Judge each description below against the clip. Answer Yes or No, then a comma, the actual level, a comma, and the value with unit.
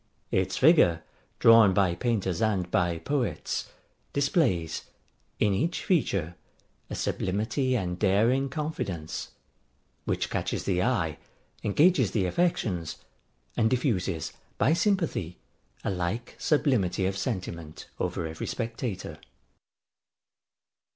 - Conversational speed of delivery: No, slow, 105 wpm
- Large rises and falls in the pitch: Yes, wide, 6.3 semitones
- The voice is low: Yes, low, 100 Hz